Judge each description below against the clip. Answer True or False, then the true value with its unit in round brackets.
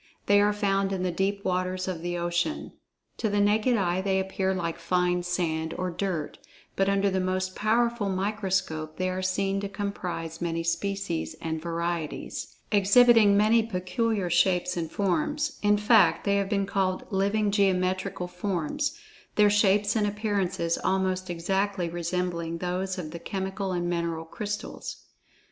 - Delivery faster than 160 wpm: False (155 wpm)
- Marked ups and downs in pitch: False (2.6 semitones)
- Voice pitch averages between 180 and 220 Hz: True (190 Hz)